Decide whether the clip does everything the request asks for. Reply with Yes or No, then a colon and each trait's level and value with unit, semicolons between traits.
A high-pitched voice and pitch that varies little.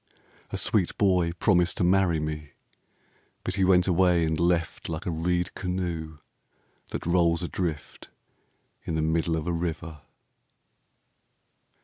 No: very low, 85 Hz; narrow, 2.0 semitones